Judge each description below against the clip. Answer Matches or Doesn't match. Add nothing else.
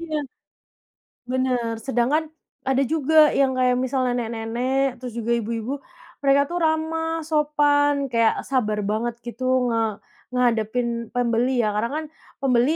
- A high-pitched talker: Matches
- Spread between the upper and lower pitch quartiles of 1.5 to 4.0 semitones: Matches